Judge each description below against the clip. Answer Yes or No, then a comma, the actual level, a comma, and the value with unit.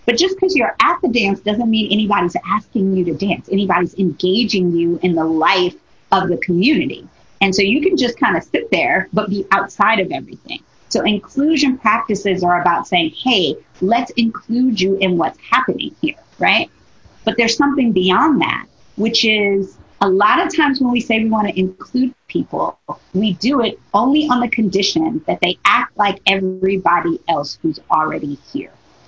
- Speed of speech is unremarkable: Yes, average, 180 wpm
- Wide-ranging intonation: No, average, 4.6 semitones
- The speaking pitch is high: Yes, high, 205 Hz